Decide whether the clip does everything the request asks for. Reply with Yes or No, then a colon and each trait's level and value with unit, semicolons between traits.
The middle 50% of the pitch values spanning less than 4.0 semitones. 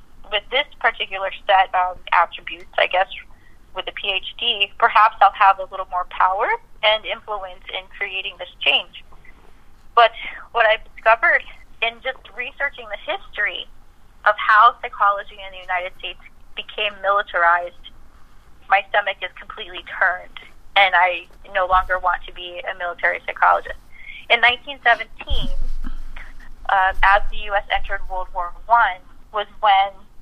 Yes: average, 3.1 semitones